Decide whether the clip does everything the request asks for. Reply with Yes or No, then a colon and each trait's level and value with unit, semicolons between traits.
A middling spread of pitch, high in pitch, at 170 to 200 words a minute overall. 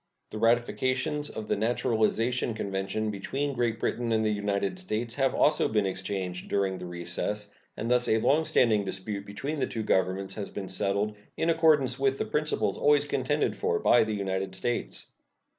No: average, 4.8 semitones; low, 110 Hz; average, 175 wpm